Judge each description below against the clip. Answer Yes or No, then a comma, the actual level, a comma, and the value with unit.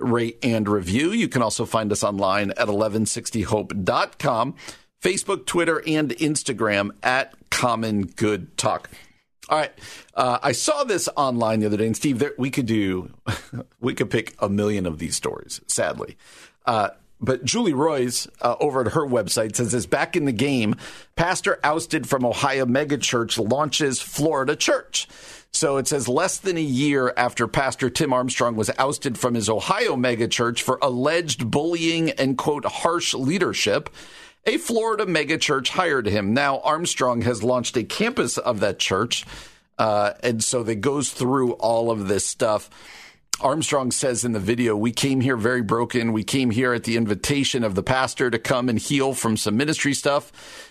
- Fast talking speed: No, average, 170 wpm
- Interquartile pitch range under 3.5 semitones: No, average, 4.1 semitones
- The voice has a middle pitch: No, low, 125 Hz